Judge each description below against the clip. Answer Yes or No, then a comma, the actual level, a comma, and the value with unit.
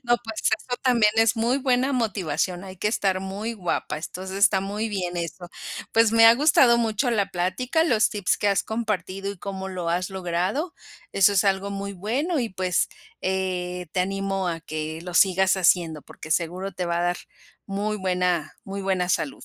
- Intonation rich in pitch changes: No, average, 3.5 semitones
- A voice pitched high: Yes, high, 195 Hz